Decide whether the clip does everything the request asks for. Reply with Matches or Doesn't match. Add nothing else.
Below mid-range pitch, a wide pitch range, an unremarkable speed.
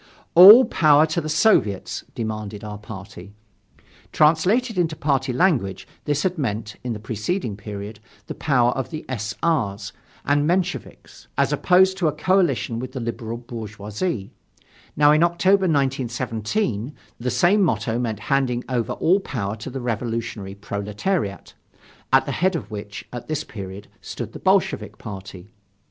Matches